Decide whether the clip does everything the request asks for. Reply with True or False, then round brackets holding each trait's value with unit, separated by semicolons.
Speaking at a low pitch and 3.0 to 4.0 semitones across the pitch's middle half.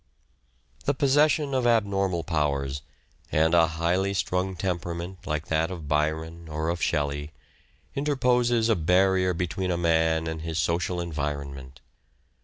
True (85 Hz; 3.4 semitones)